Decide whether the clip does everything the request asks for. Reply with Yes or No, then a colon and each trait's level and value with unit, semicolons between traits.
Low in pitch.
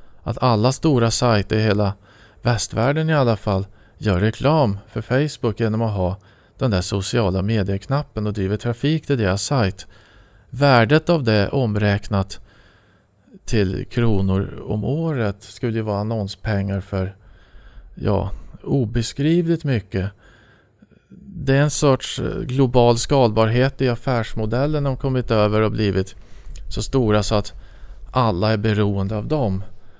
Yes: low, 110 Hz